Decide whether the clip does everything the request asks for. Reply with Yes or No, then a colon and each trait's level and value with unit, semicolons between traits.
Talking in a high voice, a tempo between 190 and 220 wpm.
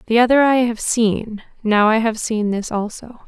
Yes: high, 225 Hz; average, 200 wpm